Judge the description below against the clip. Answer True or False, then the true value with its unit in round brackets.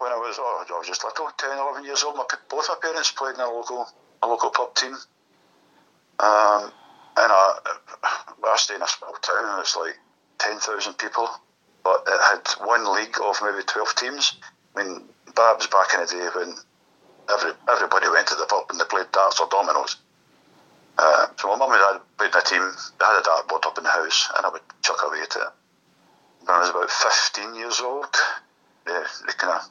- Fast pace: True (210 wpm)